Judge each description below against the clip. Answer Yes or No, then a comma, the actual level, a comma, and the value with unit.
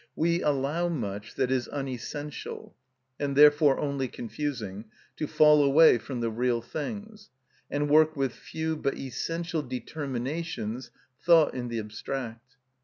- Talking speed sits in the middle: No, slow, 130 wpm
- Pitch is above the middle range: No, medium, 140 Hz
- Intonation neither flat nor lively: Yes, average, 4.0 semitones